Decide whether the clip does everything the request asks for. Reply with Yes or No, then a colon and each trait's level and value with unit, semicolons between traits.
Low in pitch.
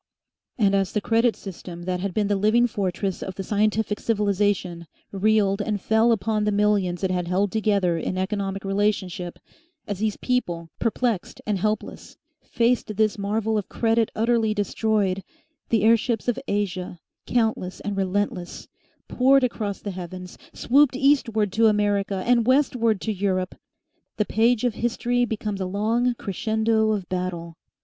No: high, 210 Hz